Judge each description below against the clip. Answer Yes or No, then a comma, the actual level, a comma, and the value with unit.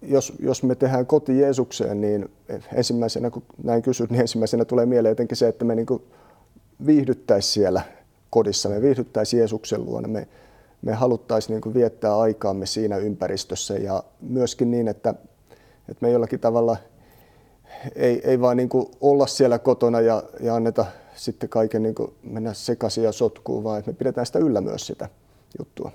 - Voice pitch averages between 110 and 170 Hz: Yes, low, 115 Hz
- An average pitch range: No, narrow, 2.2 semitones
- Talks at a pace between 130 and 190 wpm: Yes, fast, 155 wpm